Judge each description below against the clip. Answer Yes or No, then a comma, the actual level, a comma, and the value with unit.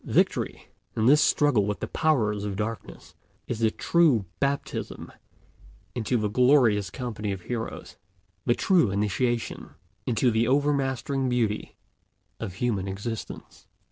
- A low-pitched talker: Yes, low, 115 Hz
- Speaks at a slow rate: Yes, slow, 125 wpm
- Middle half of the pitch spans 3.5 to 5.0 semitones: Yes, average, 4.2 semitones